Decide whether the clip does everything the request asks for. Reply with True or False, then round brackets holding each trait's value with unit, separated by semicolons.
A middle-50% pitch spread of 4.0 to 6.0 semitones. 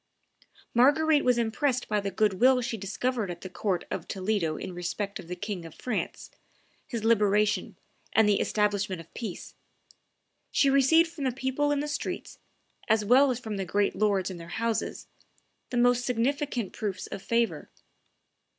True (4.3 semitones)